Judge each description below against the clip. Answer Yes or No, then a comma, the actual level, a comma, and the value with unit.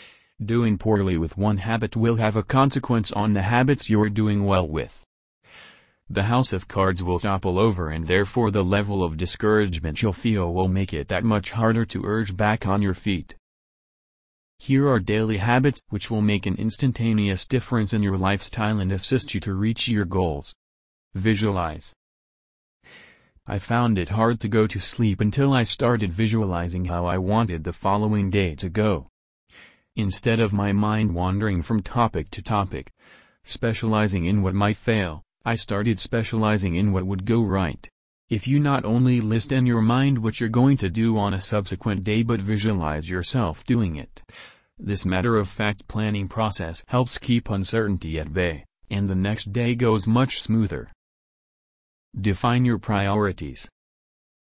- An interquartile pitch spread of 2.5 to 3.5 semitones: Yes, average, 3.2 semitones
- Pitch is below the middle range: Yes, low, 105 Hz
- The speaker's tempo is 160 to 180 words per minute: Yes, average, 165 wpm